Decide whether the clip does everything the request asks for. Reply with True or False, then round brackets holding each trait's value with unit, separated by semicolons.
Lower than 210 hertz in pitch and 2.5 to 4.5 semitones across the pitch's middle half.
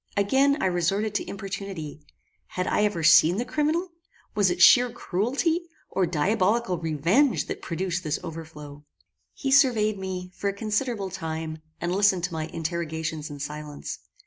False (185 Hz; 4.9 semitones)